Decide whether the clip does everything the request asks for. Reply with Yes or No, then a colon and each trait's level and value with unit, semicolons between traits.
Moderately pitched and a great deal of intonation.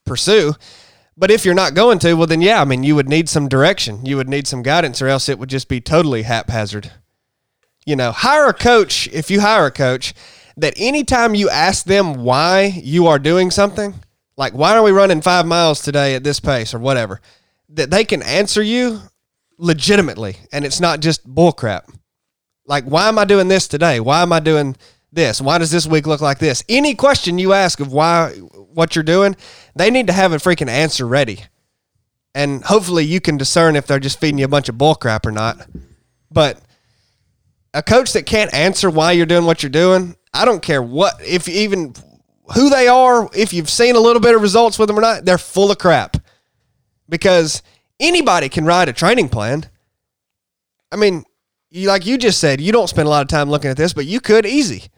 Yes: medium, 160 Hz; wide, 6.4 semitones